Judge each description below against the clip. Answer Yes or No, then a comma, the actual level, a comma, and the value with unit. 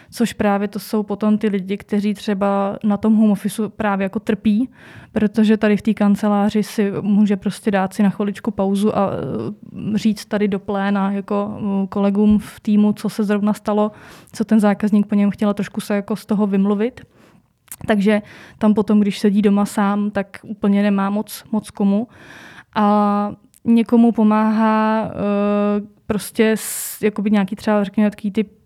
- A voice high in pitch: Yes, high, 210 Hz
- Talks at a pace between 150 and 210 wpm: Yes, average, 160 wpm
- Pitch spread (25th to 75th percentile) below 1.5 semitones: Yes, narrow, 1.1 semitones